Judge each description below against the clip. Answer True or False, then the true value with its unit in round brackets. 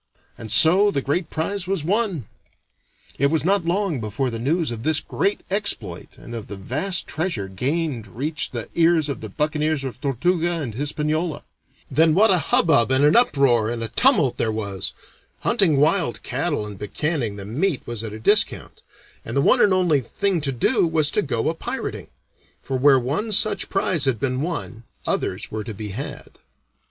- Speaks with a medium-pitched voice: True (145 Hz)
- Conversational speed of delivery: True (185 wpm)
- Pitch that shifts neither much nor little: False (6.6 semitones)